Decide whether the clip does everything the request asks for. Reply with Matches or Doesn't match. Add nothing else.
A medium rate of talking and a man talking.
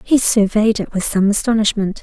Doesn't match